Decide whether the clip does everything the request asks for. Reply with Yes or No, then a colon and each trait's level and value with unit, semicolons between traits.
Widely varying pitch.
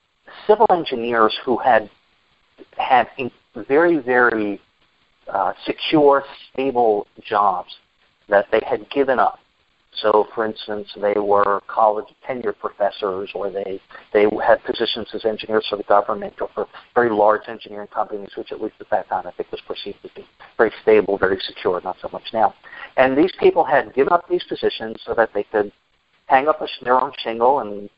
Yes: wide, 6.4 semitones